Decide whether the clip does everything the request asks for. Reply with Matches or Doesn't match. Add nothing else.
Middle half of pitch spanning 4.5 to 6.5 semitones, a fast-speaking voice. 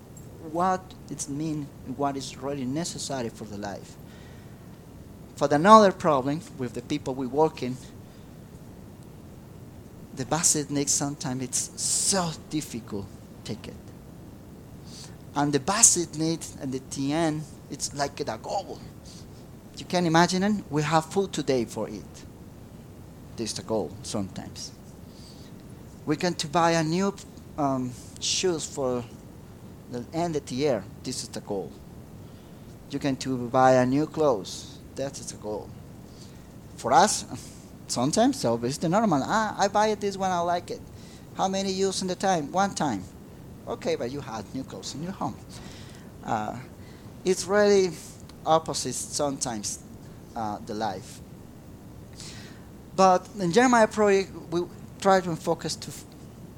Doesn't match